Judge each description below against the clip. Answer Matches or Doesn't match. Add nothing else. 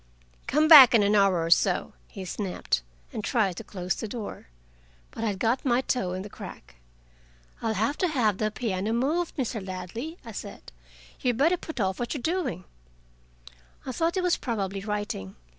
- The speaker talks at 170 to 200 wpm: Matches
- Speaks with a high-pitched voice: Matches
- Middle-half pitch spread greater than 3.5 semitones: Matches